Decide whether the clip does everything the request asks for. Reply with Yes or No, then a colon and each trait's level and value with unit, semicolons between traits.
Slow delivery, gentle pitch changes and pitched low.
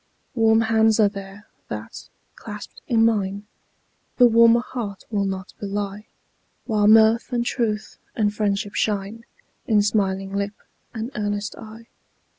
No: slow, 130 wpm; narrow, 1.9 semitones; high, 210 Hz